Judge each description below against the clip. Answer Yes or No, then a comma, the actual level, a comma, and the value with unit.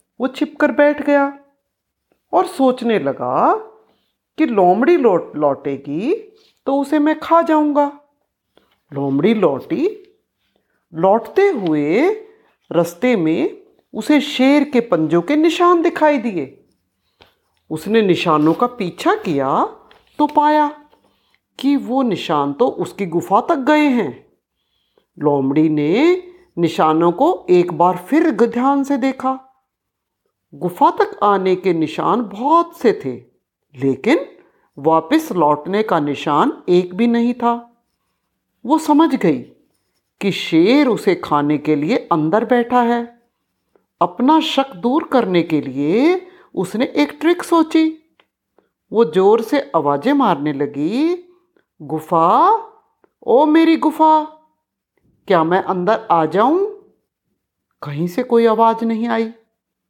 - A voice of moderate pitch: No, high, 245 Hz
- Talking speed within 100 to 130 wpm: Yes, average, 115 wpm